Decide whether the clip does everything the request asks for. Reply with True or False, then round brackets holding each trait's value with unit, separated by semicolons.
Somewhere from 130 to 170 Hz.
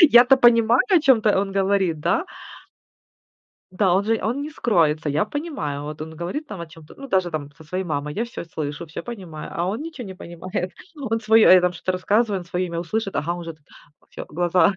False (185 Hz)